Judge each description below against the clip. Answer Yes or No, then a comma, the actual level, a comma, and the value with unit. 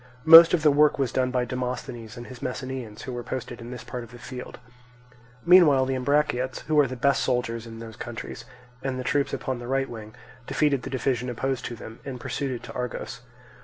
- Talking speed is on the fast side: Yes, fast, 215 wpm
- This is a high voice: No, low, 125 Hz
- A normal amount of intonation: No, narrow, 2.1 semitones